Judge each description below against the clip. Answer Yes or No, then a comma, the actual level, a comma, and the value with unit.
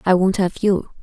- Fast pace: Yes, fast, 235 wpm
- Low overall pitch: No, high, 190 Hz